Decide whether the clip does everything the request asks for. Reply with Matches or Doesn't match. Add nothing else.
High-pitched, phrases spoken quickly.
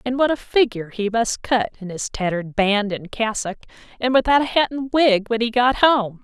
Matches